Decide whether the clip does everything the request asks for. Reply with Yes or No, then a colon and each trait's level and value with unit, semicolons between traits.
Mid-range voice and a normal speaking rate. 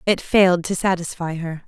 Yes: medium, 175 Hz; average, 180 wpm